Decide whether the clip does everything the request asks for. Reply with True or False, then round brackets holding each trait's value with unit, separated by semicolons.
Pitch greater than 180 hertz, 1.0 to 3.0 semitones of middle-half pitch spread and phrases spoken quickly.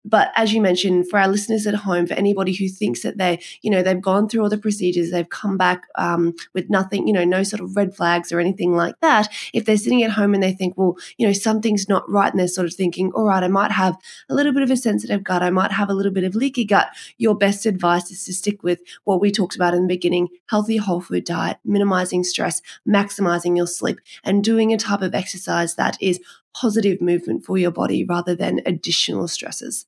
True (190 Hz; 2.6 semitones; 240 wpm)